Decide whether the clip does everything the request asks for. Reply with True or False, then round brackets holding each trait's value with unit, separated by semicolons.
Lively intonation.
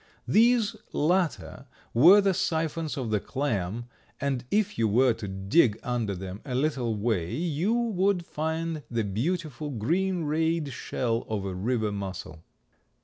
True (7.3 semitones)